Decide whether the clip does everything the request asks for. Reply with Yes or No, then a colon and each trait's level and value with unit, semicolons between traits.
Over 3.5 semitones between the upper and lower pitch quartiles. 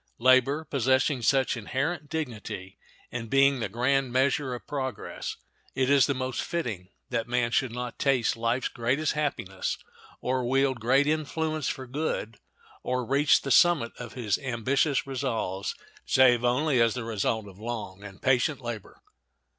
No: average, 3.0 semitones